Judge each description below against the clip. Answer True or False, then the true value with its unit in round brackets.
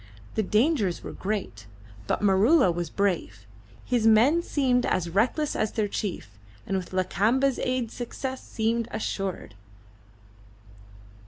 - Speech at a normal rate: False (120 wpm)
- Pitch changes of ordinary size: True (4.9 semitones)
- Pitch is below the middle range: False (215 Hz)